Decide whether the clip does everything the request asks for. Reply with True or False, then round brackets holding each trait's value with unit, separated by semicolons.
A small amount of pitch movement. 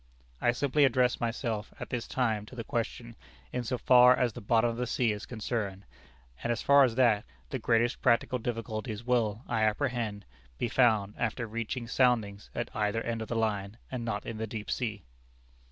True (2.3 semitones)